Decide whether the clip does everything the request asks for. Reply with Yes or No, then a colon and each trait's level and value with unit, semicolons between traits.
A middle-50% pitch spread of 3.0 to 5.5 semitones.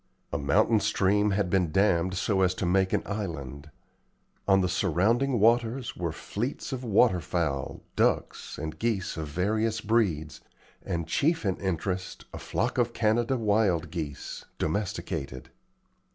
Yes: average, 4.8 semitones